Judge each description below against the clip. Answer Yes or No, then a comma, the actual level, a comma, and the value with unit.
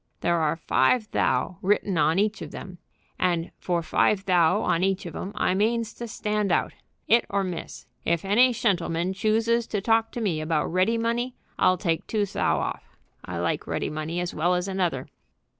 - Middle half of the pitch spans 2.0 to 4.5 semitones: Yes, average, 4.2 semitones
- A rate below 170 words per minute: No, average, 190 wpm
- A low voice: No, high, 190 Hz